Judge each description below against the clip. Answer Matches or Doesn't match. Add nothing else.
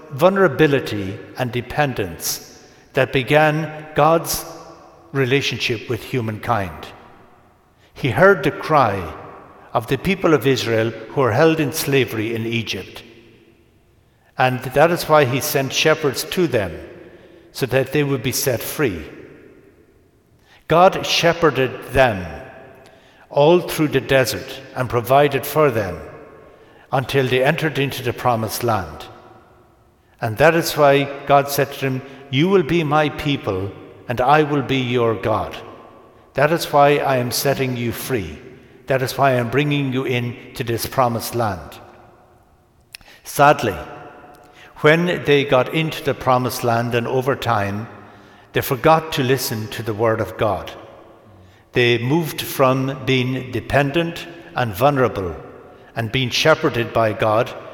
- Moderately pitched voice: Doesn't match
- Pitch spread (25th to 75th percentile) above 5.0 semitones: Doesn't match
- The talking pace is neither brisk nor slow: Doesn't match